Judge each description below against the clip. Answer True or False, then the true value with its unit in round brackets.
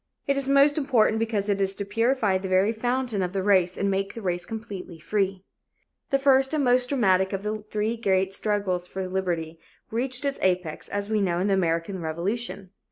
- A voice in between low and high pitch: False (200 Hz)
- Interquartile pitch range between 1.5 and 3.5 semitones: False (3.9 semitones)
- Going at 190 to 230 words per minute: True (200 wpm)